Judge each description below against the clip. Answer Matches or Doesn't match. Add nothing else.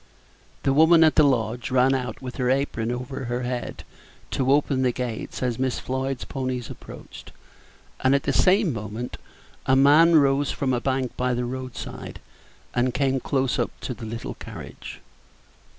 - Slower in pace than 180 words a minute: Matches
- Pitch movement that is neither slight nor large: Doesn't match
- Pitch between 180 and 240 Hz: Doesn't match